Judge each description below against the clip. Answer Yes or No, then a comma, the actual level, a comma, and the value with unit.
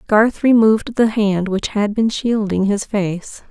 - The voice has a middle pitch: No, high, 210 Hz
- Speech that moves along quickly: No, average, 170 wpm